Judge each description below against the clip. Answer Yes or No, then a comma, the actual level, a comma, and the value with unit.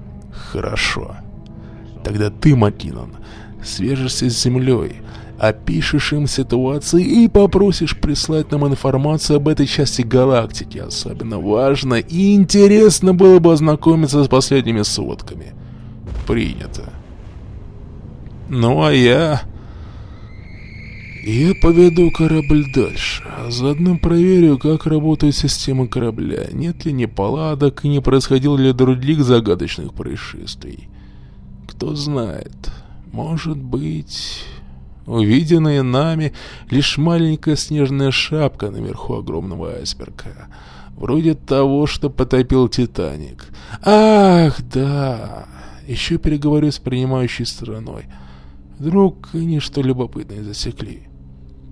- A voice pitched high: No, low, 130 Hz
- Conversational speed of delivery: No, slow, 95 wpm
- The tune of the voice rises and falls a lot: Yes, wide, 6.1 semitones